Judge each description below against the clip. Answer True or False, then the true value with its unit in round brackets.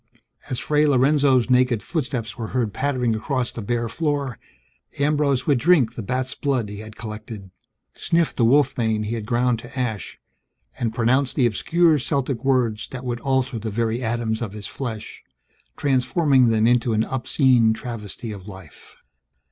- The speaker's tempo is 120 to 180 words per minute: True (160 wpm)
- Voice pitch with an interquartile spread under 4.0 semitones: True (3.4 semitones)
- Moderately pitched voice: False (125 Hz)